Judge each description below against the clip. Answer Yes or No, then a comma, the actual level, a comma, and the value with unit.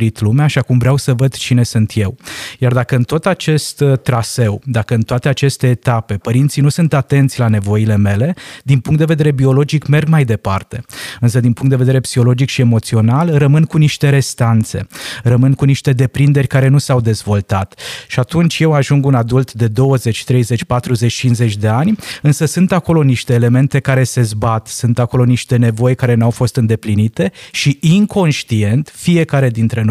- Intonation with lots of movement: No, average, 3.2 semitones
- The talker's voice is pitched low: Yes, low, 130 Hz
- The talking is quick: Yes, fast, 180 wpm